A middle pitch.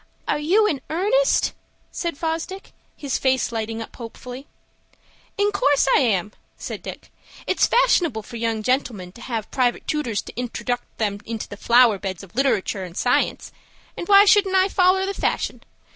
No: very high, 255 Hz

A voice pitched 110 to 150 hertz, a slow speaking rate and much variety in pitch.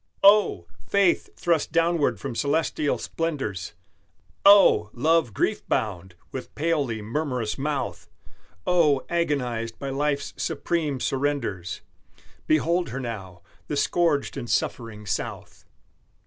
Yes: medium, 140 Hz; slow, 105 wpm; wide, 6.4 semitones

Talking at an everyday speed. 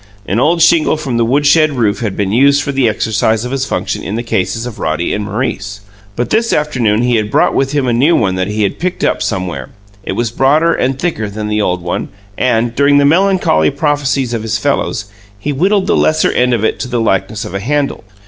No: fast, 230 wpm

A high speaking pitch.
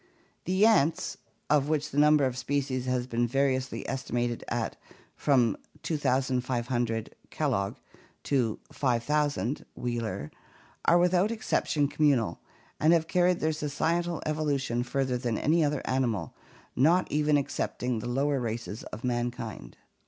No: low, 135 Hz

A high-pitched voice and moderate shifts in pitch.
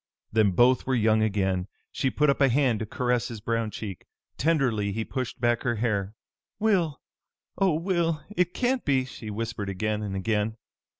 No: low, 115 Hz; average, 4.6 semitones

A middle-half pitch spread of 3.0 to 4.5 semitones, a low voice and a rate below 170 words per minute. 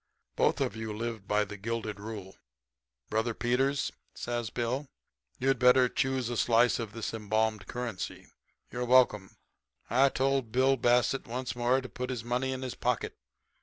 No: narrow, 2.5 semitones; low, 120 Hz; average, 160 wpm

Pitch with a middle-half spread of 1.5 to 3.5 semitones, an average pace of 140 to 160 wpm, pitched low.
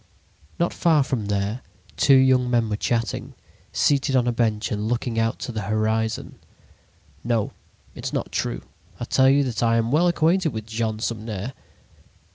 No: average, 3.2 semitones; average, 170 wpm; low, 115 Hz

